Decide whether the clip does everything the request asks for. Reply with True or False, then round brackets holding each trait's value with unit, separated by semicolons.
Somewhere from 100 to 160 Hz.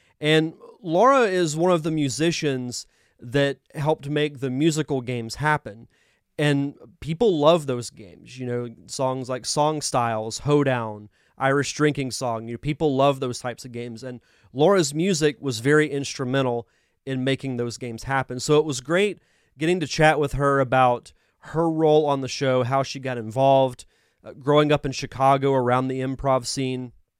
True (135 Hz)